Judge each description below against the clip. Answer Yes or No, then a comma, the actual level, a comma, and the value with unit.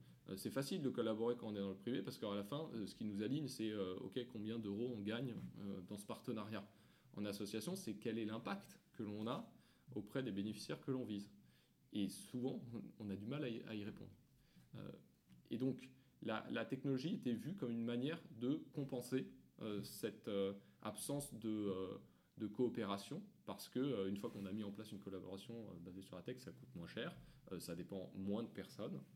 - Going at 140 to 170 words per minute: No, average, 185 wpm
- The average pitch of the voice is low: Yes, low, 110 Hz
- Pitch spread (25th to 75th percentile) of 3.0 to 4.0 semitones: Yes, average, 3.5 semitones